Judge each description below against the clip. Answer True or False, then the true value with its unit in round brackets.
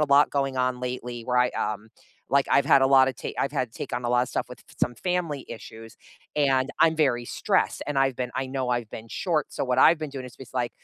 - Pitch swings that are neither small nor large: False (2.2 semitones)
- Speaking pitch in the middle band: False (130 Hz)